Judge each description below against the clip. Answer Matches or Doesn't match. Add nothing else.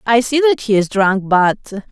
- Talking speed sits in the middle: Doesn't match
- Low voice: Doesn't match